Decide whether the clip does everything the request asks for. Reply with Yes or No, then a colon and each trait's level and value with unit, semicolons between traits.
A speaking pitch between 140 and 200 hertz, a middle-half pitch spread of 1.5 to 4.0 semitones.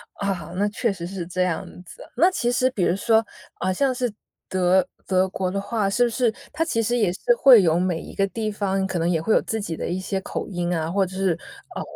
Yes: high, 195 Hz; average, 3.7 semitones